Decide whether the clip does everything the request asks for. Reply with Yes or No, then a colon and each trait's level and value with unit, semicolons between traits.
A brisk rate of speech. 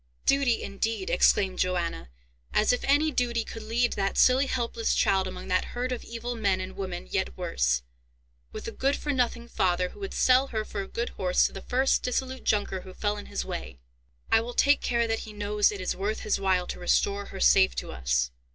Yes: fast, 215 wpm